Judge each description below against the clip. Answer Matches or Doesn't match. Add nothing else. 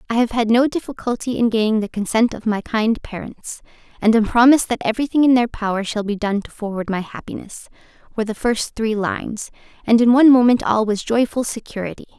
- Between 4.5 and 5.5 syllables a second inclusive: Doesn't match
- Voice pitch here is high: Matches